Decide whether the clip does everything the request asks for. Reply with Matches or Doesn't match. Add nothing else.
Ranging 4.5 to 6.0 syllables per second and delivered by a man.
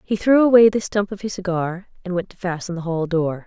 Doesn't match